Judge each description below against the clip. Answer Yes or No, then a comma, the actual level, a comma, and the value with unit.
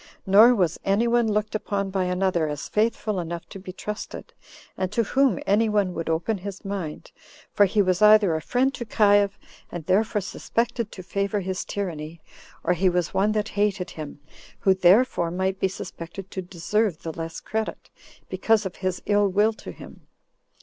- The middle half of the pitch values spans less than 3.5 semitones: Yes, average, 2.9 semitones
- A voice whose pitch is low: No, high, 195 Hz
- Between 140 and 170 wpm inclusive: No, average, 180 wpm